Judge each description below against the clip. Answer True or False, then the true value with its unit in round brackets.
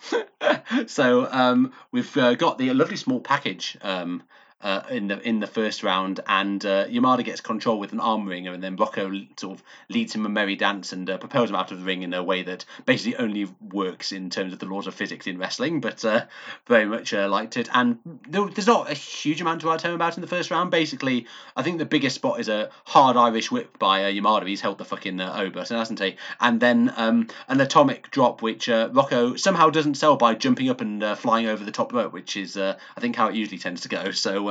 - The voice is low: True (120 Hz)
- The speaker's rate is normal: False (240 wpm)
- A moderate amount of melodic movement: False (8.5 semitones)